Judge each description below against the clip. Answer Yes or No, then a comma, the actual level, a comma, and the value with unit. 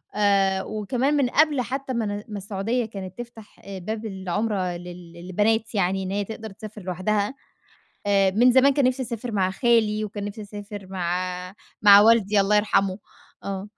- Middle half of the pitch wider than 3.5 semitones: No, average, 2.8 semitones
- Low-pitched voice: No, high, 205 Hz